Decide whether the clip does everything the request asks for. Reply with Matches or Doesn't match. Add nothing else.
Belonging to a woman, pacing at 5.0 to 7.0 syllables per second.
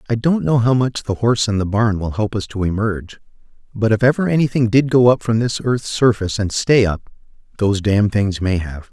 Doesn't match